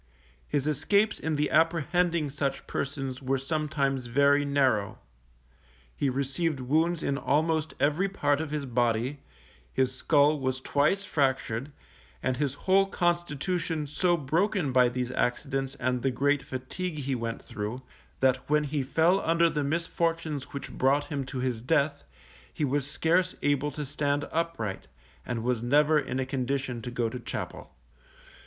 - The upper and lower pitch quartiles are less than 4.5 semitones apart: Yes, average, 3.4 semitones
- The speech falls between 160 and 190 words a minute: No, average, 150 wpm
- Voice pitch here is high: No, medium, 145 Hz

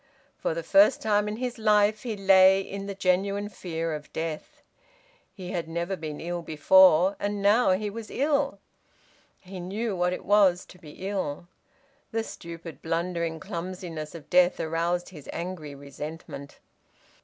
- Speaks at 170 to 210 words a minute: No, average, 155 wpm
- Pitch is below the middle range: No, medium, 185 Hz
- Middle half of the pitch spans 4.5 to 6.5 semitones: No, average, 3.6 semitones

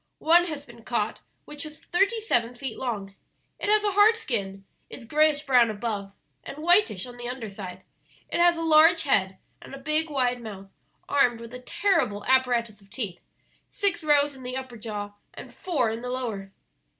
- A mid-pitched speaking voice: No, very high, 250 Hz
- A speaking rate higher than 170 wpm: Yes, average, 185 wpm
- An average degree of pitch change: No, wide, 5.9 semitones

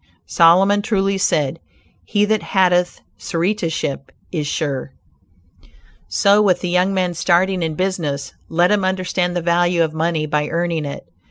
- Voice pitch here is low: No, medium, 175 Hz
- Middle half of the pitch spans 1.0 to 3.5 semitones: Yes, average, 2.9 semitones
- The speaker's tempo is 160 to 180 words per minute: No, average, 145 wpm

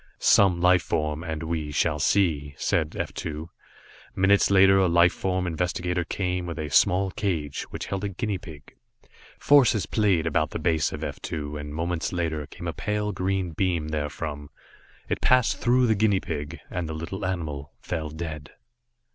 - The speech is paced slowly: No, average, 170 wpm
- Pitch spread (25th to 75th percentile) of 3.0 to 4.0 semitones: Yes, average, 3.7 semitones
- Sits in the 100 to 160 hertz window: No, very low, 85 Hz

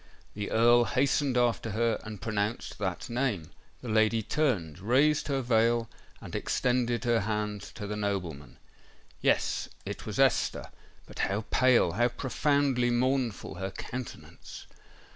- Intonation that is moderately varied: Yes, average, 3.3 semitones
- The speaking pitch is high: No, low, 115 Hz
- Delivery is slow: Yes, slow, 115 wpm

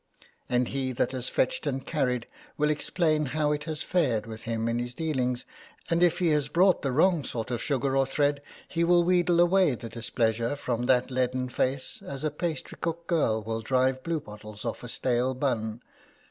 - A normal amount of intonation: Yes, average, 4.3 semitones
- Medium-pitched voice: No, low, 130 Hz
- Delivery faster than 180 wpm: Yes, average, 190 wpm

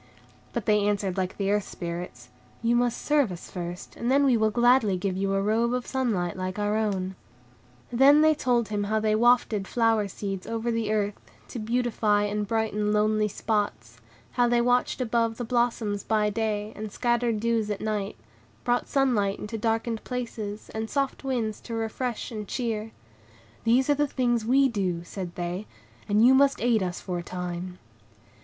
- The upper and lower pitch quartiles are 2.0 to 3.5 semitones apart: Yes, average, 3.0 semitones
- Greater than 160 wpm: Yes, average, 180 wpm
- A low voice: No, high, 220 Hz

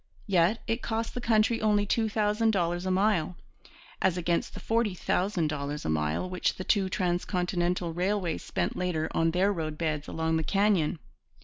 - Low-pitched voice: No, medium, 180 Hz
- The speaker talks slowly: No, average, 170 wpm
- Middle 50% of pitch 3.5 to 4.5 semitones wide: Yes, average, 4.0 semitones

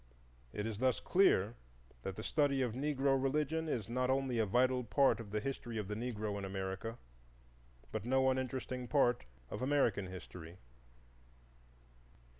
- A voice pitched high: No, low, 125 Hz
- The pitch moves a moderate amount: Yes, average, 4.1 semitones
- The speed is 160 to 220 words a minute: No, average, 150 wpm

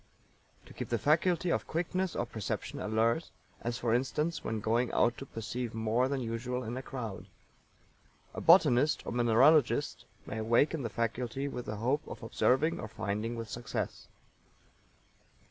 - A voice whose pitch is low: Yes, low, 120 Hz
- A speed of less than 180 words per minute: Yes, average, 155 wpm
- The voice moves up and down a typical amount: Yes, average, 3.9 semitones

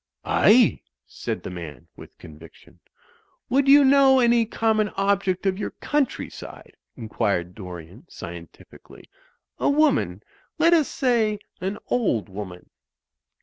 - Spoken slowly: Yes, slow, 120 wpm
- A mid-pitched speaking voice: No, high, 195 Hz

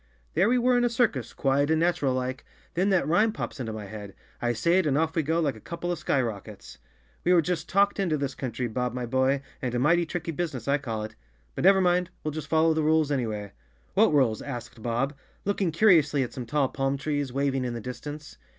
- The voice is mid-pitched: Yes, medium, 145 Hz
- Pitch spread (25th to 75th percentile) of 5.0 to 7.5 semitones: Yes, average, 5.3 semitones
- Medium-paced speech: No, fast, 240 wpm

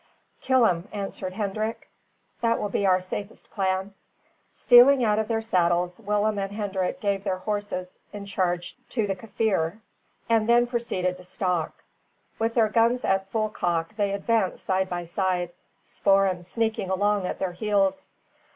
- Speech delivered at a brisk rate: No, average, 155 wpm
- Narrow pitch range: No, average, 3.1 semitones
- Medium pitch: No, high, 200 Hz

